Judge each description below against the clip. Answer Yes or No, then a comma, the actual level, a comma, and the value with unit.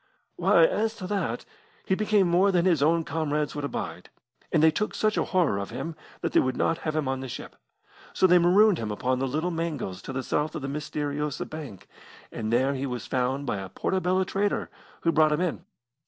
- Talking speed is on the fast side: Yes, fast, 215 wpm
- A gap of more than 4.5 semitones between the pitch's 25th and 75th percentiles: Yes, average, 5.2 semitones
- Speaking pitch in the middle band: Yes, medium, 155 Hz